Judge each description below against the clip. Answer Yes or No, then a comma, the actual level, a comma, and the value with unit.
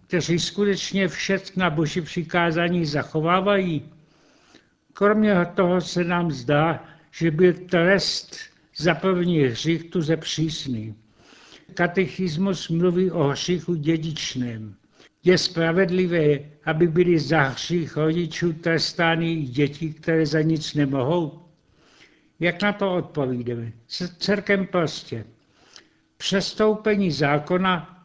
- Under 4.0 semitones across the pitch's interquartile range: Yes, average, 2.8 semitones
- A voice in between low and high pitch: Yes, medium, 170 Hz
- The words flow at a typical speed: No, slow, 105 wpm